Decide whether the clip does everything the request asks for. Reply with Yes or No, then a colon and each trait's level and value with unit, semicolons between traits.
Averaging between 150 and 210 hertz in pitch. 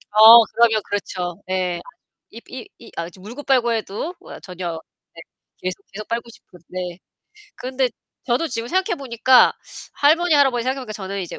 No: high, 230 Hz